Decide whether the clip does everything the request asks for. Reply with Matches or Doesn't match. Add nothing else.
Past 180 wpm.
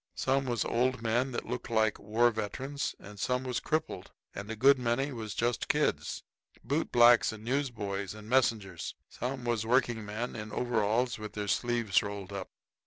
Doesn't match